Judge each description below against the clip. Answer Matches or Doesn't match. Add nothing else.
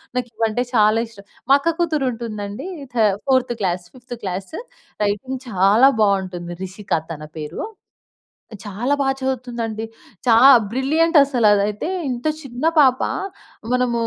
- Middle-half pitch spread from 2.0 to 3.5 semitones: Doesn't match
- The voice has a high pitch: Matches